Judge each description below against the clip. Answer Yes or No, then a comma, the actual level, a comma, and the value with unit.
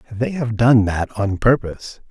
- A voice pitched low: Yes, low, 110 Hz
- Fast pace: No, average, 170 wpm